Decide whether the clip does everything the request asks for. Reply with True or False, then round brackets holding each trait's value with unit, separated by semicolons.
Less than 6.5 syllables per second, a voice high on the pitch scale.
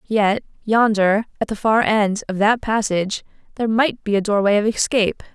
True (5.2 syllables/s; 210 Hz)